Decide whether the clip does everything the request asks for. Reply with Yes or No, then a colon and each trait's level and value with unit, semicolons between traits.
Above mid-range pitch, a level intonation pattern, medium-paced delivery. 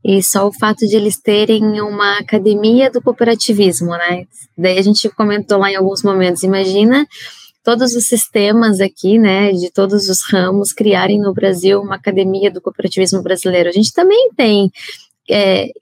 Yes: high, 200 Hz; narrow, 2.2 semitones; average, 165 wpm